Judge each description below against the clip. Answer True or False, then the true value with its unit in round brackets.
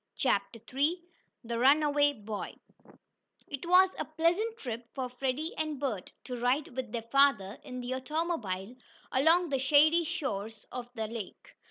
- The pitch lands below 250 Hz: False (265 Hz)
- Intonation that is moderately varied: True (4.9 semitones)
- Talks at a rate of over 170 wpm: False (150 wpm)